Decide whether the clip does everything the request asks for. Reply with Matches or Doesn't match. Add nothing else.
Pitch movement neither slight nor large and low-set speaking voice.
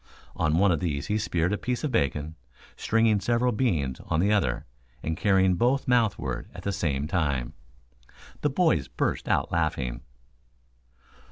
Doesn't match